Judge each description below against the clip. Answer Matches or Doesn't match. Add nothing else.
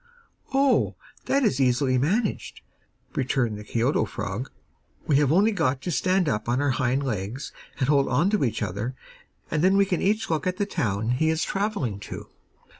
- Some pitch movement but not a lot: Doesn't match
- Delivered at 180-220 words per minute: Matches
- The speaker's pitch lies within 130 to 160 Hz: Matches